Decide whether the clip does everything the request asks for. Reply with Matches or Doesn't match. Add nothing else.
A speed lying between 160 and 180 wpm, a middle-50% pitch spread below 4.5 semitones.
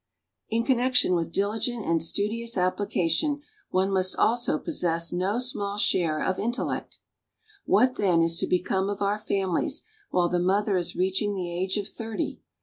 Matches